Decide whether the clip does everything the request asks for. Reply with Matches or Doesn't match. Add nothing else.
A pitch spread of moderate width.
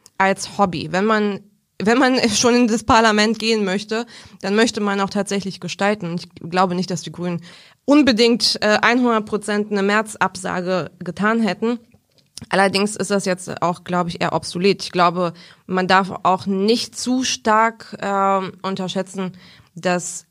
Matches